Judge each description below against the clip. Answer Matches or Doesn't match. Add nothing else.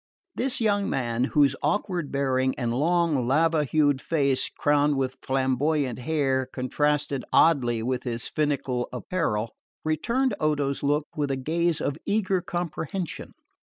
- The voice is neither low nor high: Matches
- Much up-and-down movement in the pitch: Doesn't match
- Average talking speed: Doesn't match